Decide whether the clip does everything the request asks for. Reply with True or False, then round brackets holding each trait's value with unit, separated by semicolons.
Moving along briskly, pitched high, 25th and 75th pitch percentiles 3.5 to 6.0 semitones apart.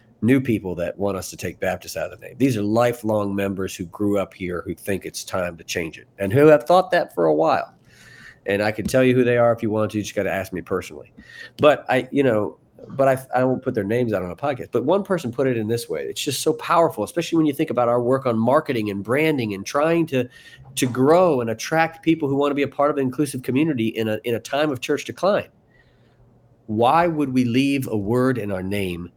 False (260 wpm; 125 Hz; 4.8 semitones)